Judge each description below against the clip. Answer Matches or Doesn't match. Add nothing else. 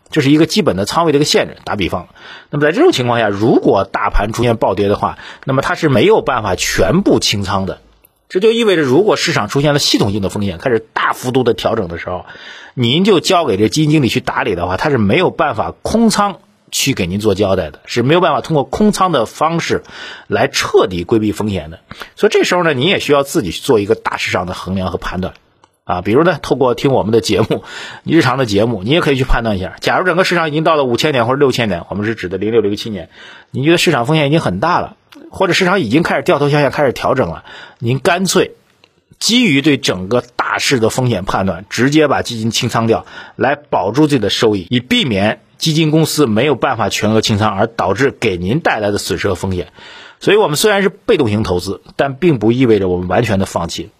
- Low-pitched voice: Matches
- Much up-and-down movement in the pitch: Matches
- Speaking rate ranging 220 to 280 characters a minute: Doesn't match